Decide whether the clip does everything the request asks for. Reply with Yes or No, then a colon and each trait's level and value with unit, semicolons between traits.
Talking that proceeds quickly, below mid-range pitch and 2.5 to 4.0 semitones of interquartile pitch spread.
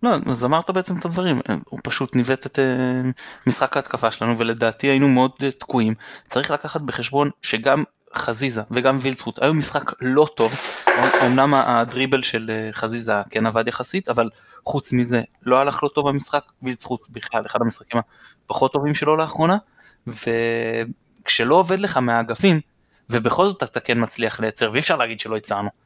Yes: fast, 155 wpm; low, 125 Hz; average, 3.6 semitones